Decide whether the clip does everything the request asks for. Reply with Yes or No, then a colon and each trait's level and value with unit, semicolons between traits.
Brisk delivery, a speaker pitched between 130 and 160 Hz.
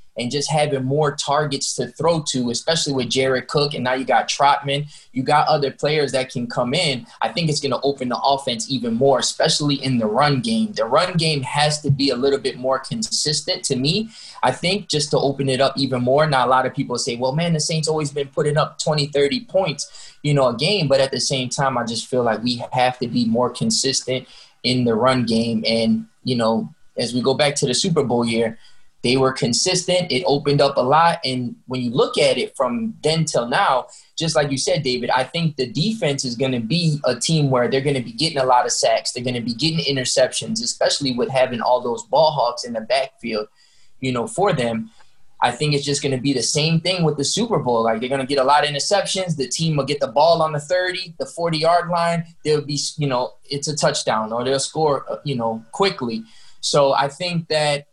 Yes: fast, 240 wpm; medium, 140 Hz